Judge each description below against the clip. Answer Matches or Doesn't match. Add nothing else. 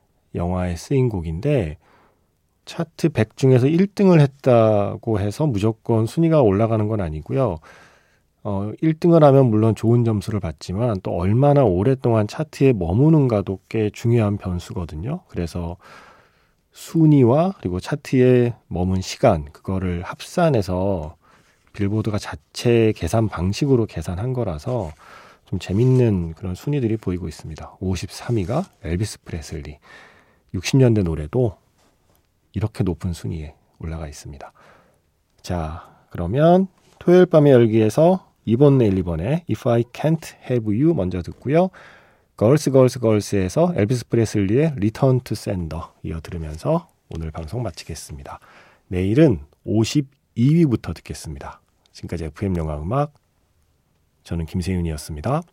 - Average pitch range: Doesn't match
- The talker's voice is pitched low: Matches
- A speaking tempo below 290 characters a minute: Doesn't match